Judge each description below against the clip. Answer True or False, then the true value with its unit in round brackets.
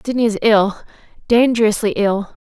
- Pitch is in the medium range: False (215 Hz)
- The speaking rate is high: False (100 wpm)